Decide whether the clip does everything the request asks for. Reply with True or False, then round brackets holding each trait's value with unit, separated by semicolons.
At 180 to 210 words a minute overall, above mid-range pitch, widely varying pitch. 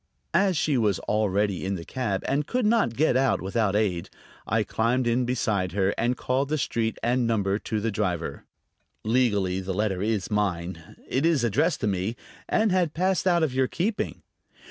False (185 wpm; 115 Hz; 5.7 semitones)